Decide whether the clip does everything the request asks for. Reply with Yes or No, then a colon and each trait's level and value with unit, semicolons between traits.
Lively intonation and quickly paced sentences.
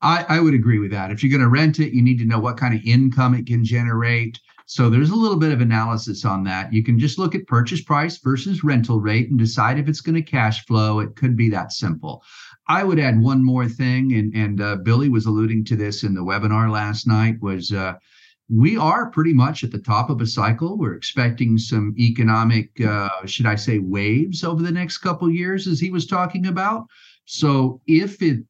Yes: wide, 5.7 semitones; fast, 230 wpm